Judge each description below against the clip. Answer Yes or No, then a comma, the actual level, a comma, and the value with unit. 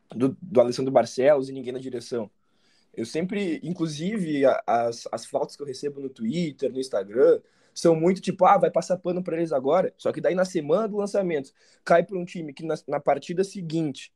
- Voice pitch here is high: No, medium, 165 Hz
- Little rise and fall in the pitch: No, wide, 5.6 semitones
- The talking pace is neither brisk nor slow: No, fast, 200 wpm